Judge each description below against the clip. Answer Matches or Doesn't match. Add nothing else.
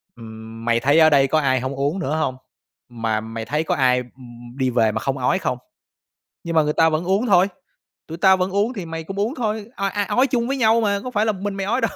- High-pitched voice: Doesn't match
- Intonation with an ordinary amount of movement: Doesn't match